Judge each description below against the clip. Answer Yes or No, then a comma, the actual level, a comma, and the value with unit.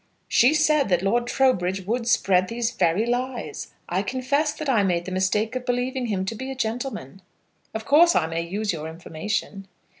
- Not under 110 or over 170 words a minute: No, average, 185 wpm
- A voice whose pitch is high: Yes, high, 220 Hz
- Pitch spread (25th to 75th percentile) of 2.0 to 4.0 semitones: No, wide, 5.5 semitones